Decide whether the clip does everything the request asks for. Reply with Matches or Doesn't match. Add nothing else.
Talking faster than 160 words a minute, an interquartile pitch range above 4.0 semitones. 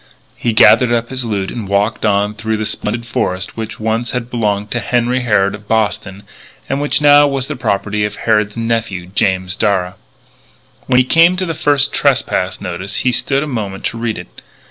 Doesn't match